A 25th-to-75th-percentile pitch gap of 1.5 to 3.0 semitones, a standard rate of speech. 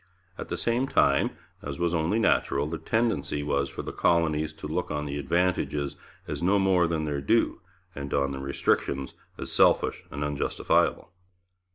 No: average, 3.8 semitones; average, 170 wpm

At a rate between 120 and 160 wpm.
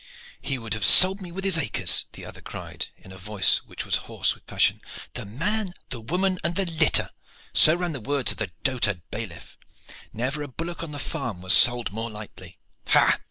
No: fast, 205 wpm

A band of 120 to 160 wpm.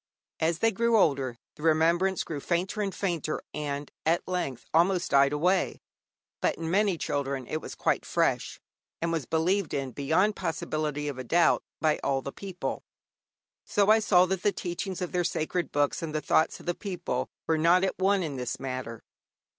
No: average, 185 wpm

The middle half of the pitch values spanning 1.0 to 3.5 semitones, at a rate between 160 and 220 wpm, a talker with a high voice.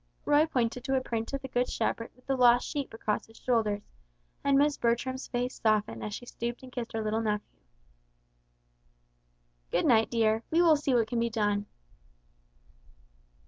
Yes: average, 2.9 semitones; average, 175 wpm; high, 240 Hz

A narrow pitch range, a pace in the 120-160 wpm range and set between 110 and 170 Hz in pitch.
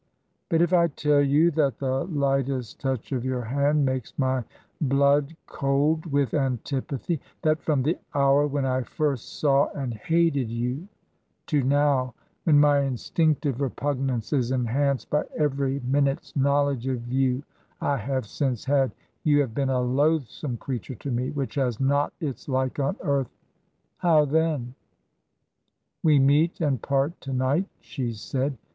Yes: narrow, 2.1 semitones; average, 150 wpm; medium, 140 Hz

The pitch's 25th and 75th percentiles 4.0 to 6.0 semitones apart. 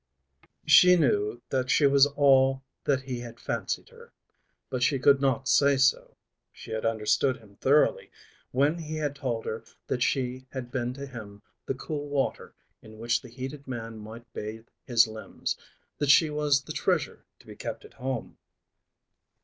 No: average, 3.2 semitones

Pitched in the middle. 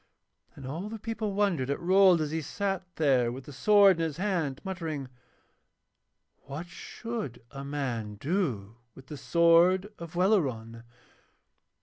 Yes: medium, 160 Hz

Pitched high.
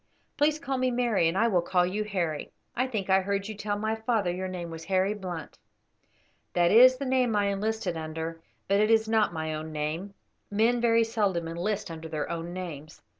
Yes: high, 195 Hz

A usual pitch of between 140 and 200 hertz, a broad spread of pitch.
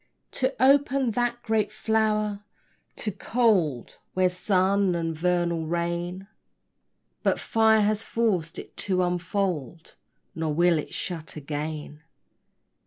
No: medium, 185 Hz; average, 4.4 semitones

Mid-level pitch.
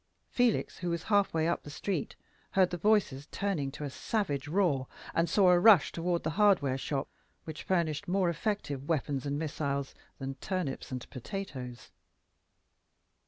Yes: medium, 165 Hz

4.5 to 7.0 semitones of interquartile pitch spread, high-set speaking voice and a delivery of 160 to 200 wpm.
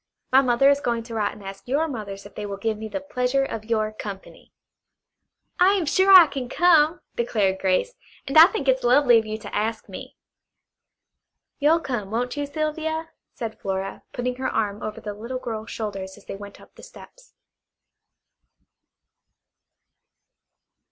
Yes: average, 5.3 semitones; high, 240 Hz; average, 170 wpm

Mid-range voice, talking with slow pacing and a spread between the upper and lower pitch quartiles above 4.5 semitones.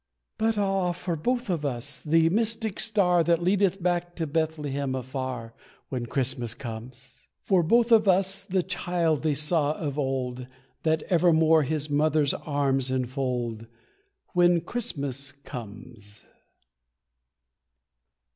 Yes: medium, 155 Hz; slow, 120 wpm; average, 5.3 semitones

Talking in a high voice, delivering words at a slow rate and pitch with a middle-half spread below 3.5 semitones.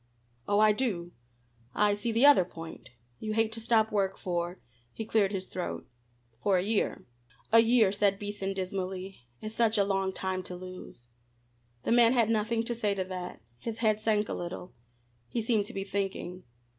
No: high, 205 Hz; average, 180 wpm; average, 2.9 semitones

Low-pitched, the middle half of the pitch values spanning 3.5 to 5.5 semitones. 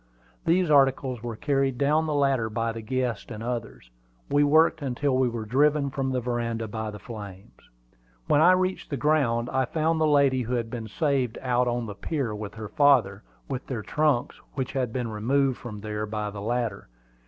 Yes: low, 125 Hz; average, 3.9 semitones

